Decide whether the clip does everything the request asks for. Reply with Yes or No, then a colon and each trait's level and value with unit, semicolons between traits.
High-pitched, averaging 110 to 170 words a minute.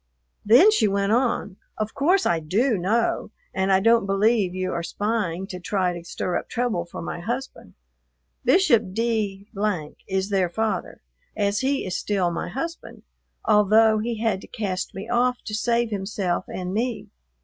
Yes: high, 210 Hz; average, 165 wpm